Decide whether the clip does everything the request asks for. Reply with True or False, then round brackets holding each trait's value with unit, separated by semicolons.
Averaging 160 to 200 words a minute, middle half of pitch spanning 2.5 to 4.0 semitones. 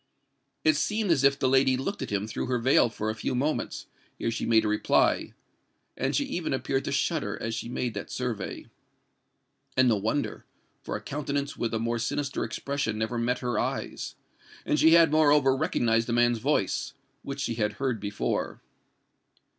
True (180 wpm; 3.7 semitones)